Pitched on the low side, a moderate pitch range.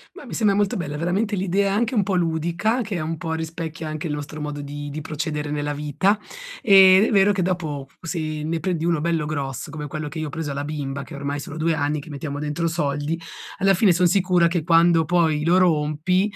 No: medium, 160 Hz; average, 3.5 semitones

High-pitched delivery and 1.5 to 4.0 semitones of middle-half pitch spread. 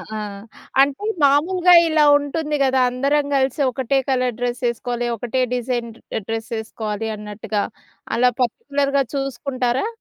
Yes: very high, 255 Hz; average, 3.0 semitones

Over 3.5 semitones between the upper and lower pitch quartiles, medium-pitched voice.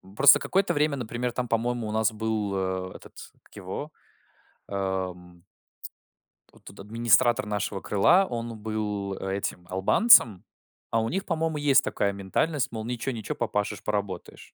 No: average, 4.0 semitones; low, 110 Hz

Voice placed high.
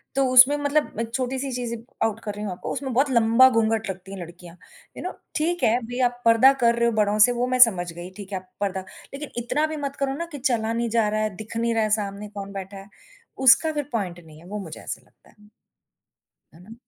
Yes: high, 230 Hz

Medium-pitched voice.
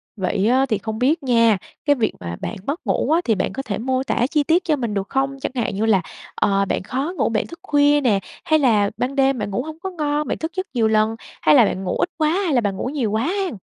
No: very high, 255 Hz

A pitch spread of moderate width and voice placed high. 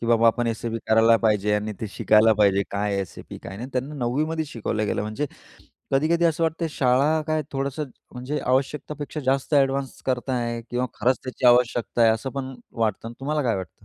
No: average, 3.7 semitones; low, 125 Hz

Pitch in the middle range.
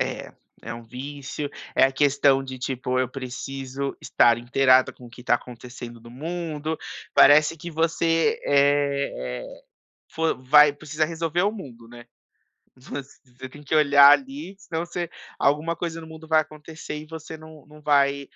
Yes: medium, 145 Hz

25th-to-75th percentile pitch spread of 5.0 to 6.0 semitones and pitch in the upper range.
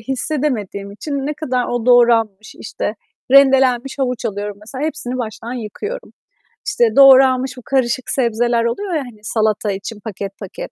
No: average, 3.7 semitones; high, 245 Hz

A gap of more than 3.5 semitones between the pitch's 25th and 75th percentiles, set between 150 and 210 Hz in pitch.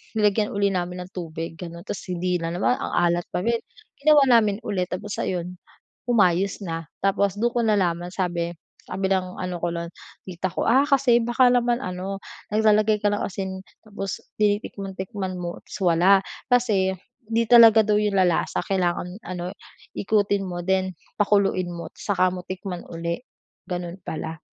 No: average, 2.9 semitones; high, 190 Hz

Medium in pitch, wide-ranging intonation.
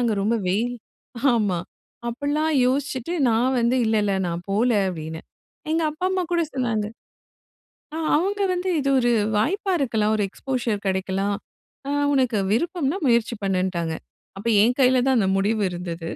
No: high, 235 Hz; wide, 5.8 semitones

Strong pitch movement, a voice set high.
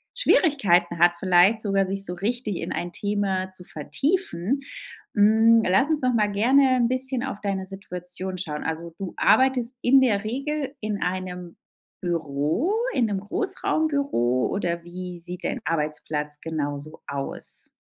Yes: wide, 6.0 semitones; high, 195 Hz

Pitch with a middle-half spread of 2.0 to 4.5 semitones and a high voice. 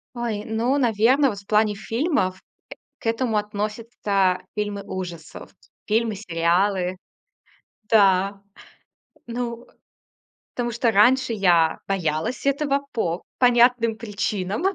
Yes: average, 3.6 semitones; high, 215 Hz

